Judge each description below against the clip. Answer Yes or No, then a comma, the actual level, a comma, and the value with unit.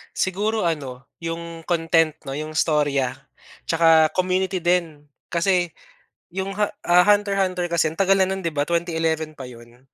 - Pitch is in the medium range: Yes, medium, 170 Hz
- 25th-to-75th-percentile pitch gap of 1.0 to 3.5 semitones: Yes, average, 3.1 semitones